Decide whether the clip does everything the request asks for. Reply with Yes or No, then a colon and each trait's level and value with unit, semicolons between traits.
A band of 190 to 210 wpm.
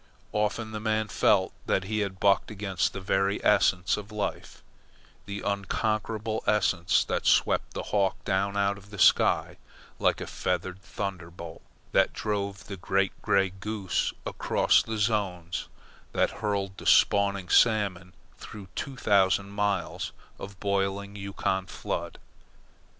No: slow, 135 wpm